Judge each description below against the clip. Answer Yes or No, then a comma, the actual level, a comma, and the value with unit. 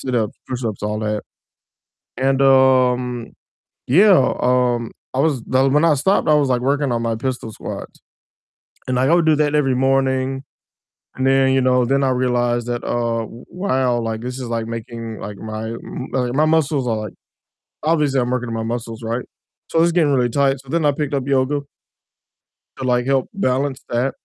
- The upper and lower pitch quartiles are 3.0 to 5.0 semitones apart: No, narrow, 2.5 semitones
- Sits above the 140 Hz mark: No, low, 130 Hz